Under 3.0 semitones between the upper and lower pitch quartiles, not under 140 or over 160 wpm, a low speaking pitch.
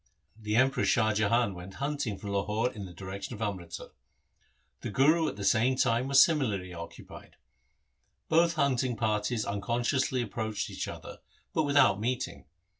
No: average, 4.6 semitones; average, 155 wpm; low, 115 Hz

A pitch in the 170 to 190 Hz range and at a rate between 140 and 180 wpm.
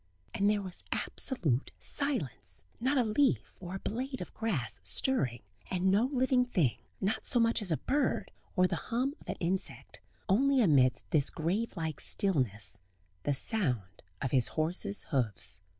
Yes: medium, 185 Hz; average, 160 wpm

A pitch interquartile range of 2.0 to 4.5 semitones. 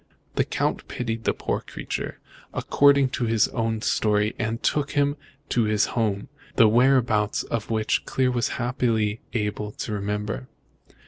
Yes: average, 2.8 semitones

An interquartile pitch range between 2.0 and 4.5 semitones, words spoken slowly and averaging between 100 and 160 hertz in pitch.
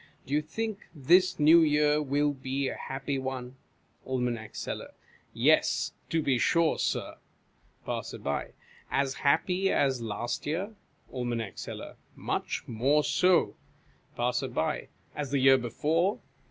Yes: average, 3.5 semitones; slow, 125 wpm; medium, 140 Hz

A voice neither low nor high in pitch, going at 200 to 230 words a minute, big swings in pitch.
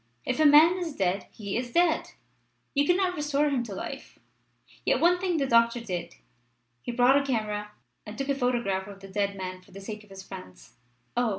No: high, 240 Hz; fast, 205 wpm; wide, 6.5 semitones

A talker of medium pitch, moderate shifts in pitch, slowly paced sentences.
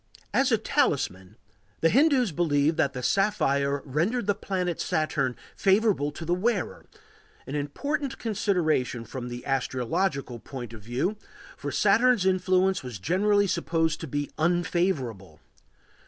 No: medium, 165 Hz; wide, 6.7 semitones; slow, 130 wpm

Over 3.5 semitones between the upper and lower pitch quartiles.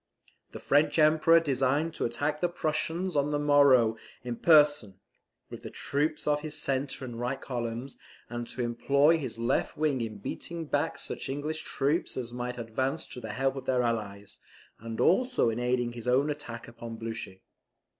Yes: average, 4.0 semitones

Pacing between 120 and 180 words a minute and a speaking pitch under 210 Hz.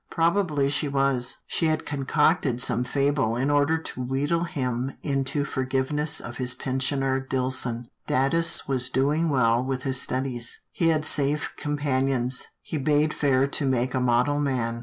Yes: average, 155 wpm; low, 135 Hz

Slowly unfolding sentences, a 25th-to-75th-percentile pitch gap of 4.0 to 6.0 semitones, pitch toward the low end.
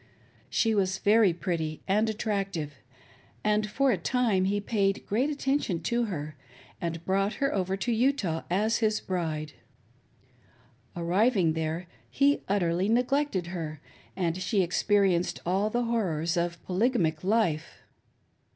No: slow, 130 wpm; average, 4.5 semitones; high, 195 Hz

